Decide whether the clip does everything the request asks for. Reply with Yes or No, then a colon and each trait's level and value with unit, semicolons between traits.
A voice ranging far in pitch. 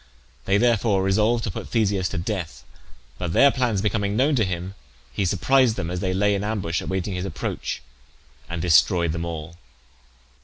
No: average, 3.8 semitones